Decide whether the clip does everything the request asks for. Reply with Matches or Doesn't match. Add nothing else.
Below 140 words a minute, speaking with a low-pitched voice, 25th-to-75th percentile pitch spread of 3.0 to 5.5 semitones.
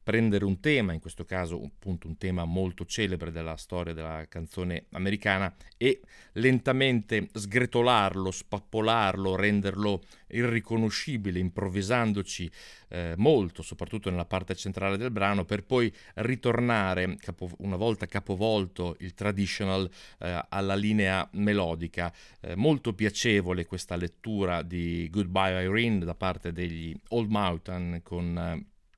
Matches